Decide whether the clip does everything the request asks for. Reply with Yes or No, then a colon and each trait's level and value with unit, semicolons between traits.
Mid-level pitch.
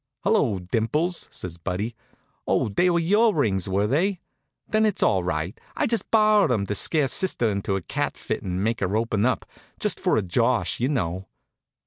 No: low, 115 Hz